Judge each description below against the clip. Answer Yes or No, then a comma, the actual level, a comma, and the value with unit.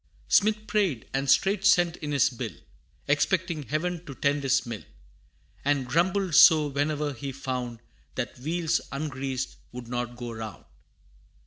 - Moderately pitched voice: Yes, medium, 145 Hz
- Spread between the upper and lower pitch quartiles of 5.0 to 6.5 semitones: No, average, 4.6 semitones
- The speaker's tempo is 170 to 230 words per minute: No, average, 140 wpm